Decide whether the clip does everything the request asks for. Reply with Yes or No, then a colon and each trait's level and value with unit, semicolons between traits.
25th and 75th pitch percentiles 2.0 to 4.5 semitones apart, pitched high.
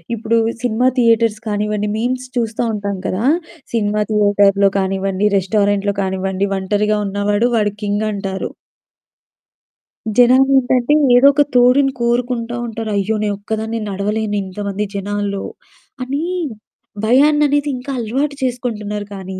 Yes: average, 3.3 semitones; high, 215 Hz